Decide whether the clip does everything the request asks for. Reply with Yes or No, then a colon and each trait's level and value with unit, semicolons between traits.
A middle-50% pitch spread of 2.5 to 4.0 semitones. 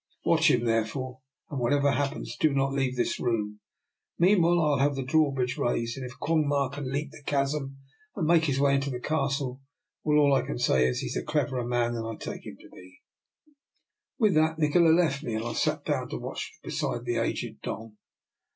Yes: average, 3.6 semitones